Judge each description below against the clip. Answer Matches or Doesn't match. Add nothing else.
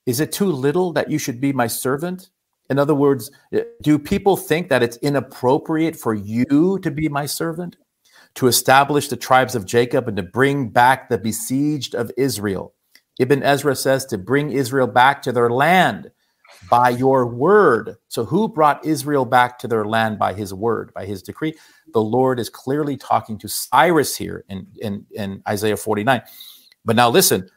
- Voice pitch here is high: Doesn't match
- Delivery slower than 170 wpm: Doesn't match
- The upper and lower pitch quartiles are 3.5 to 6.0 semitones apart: Matches